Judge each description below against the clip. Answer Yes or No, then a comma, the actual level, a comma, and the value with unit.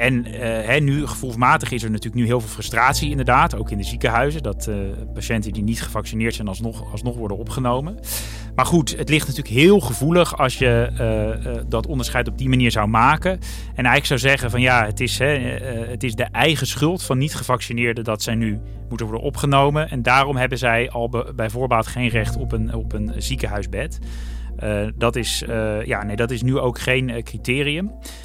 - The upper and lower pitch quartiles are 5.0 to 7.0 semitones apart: No, average, 2.9 semitones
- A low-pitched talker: Yes, low, 120 Hz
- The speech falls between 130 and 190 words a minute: No, fast, 200 wpm